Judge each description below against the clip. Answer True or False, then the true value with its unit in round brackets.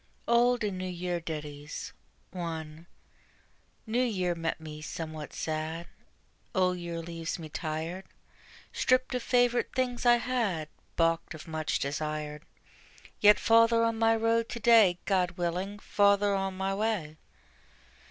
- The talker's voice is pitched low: False (180 Hz)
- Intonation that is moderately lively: False (5.9 semitones)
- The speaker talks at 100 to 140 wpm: True (135 wpm)